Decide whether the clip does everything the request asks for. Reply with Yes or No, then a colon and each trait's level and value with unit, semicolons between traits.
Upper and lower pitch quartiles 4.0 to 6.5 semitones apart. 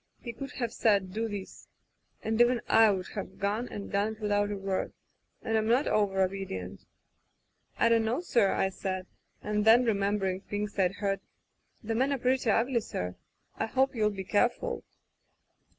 No: average, 2.9 semitones